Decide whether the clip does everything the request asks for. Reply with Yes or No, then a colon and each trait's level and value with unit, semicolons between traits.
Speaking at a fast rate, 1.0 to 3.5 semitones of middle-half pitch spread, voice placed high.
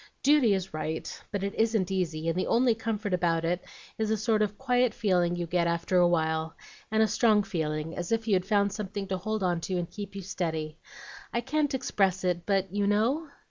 No: fast, 215 wpm; average, 4.0 semitones; high, 195 Hz